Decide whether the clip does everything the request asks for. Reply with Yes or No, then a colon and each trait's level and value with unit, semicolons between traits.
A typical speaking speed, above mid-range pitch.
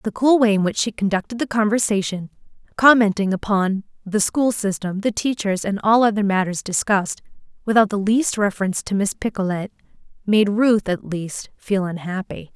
Yes: average, 160 wpm; high, 205 Hz